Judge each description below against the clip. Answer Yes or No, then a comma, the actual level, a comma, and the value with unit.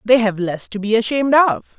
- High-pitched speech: Yes, high, 225 Hz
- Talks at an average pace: No, fast, 235 wpm